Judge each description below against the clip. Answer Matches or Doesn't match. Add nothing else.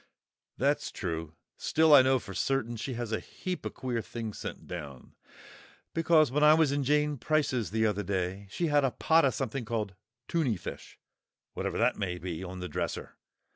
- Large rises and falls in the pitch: Matches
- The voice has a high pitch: Doesn't match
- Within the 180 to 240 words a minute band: Matches